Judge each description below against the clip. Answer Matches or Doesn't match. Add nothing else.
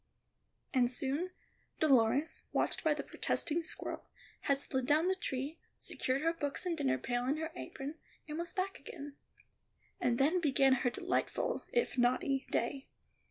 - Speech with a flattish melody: Doesn't match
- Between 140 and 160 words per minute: Matches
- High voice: Matches